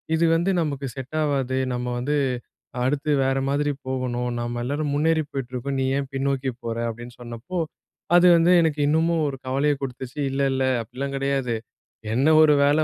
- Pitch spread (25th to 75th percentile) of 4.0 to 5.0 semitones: No, average, 2.7 semitones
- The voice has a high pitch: No, low, 135 Hz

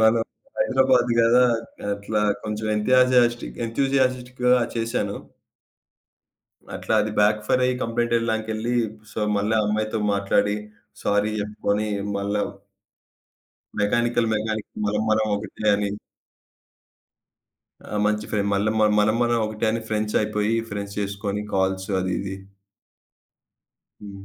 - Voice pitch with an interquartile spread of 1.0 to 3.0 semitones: Yes, narrow, 2.4 semitones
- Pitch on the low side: Yes, low, 110 Hz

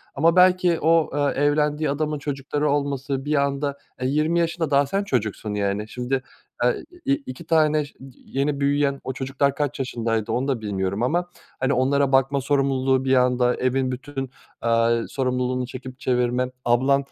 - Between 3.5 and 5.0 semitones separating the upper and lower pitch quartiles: No, narrow, 2.5 semitones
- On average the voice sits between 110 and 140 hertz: Yes, low, 135 Hz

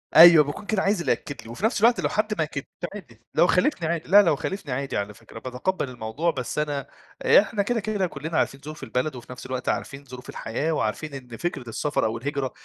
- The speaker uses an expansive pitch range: Yes, wide, 6.0 semitones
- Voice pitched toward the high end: No, medium, 145 Hz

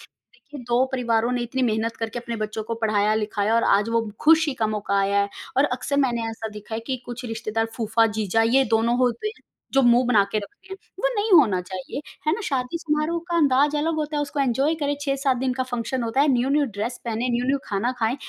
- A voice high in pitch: Yes, high, 240 Hz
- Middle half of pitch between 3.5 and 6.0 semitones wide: Yes, average, 3.9 semitones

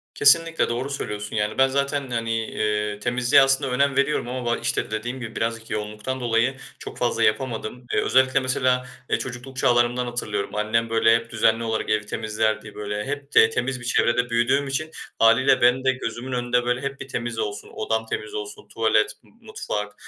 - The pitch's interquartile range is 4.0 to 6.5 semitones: No, average, 3.0 semitones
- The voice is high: No, low, 120 Hz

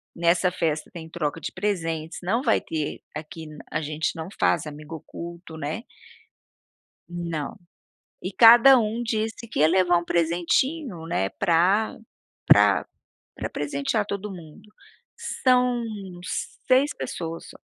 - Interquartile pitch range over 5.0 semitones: Yes, wide, 5.4 semitones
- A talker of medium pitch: Yes, medium, 175 Hz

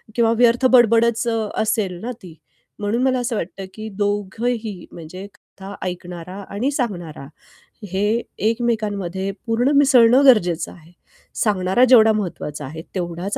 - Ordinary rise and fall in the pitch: Yes, average, 4.3 semitones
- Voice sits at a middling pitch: No, high, 210 Hz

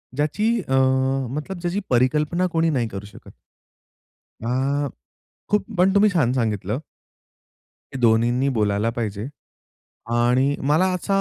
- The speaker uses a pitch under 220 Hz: Yes, low, 135 Hz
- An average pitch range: No, wide, 6.0 semitones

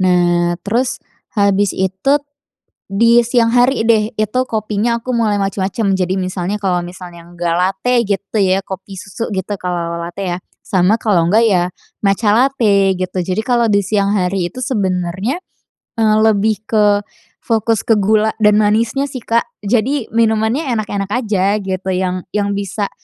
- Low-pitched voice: No, high, 205 Hz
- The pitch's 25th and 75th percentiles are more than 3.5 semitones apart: No, average, 3.2 semitones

